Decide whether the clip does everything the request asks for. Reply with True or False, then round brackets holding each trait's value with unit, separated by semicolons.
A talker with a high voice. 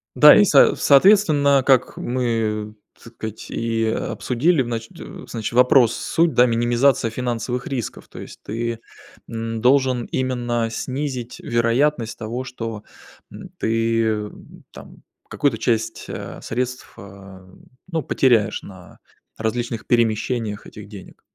False (115 Hz)